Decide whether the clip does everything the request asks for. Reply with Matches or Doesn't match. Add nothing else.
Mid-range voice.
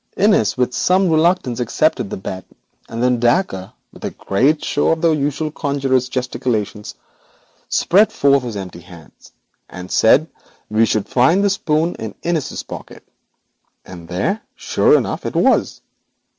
Doesn't match